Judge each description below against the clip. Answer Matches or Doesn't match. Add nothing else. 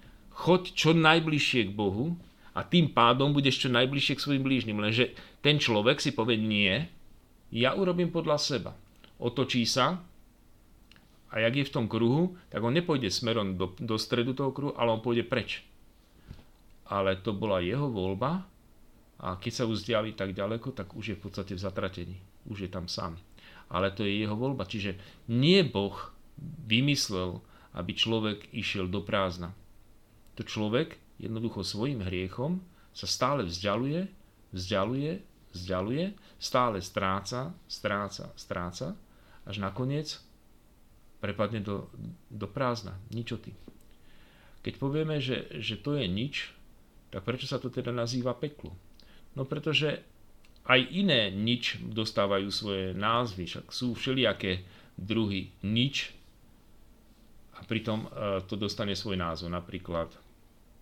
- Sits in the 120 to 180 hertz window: Doesn't match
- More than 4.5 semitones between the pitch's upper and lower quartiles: Matches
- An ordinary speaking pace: Matches